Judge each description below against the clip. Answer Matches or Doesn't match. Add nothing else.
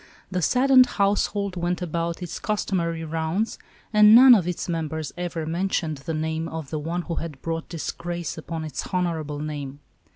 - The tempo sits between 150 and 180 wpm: Matches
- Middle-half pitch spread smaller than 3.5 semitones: Matches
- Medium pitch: Matches